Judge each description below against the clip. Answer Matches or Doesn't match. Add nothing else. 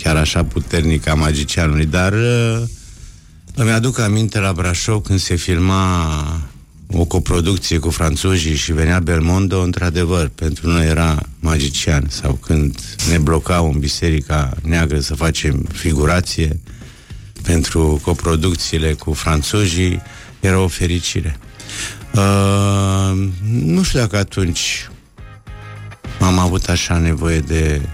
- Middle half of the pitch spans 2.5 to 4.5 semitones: Matches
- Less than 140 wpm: Matches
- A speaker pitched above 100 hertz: Doesn't match